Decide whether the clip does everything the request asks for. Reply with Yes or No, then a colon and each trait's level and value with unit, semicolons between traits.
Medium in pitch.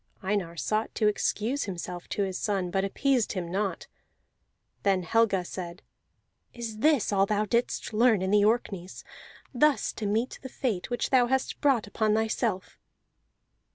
No: high, 210 Hz